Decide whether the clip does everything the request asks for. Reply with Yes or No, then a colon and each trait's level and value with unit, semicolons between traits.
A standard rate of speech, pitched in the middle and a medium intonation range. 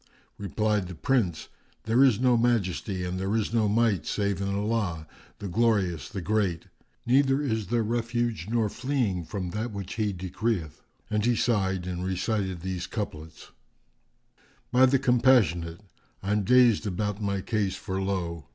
No: average, 150 wpm; low, 105 Hz; average, 4.0 semitones